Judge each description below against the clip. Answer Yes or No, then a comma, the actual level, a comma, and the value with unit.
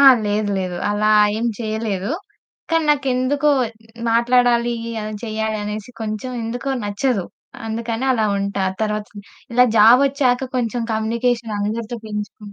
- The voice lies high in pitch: Yes, high, 225 Hz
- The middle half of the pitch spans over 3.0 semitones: No, average, 2.7 semitones